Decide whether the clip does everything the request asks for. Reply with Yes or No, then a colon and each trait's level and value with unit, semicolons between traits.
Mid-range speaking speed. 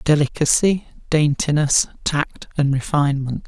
No: slow, 85 wpm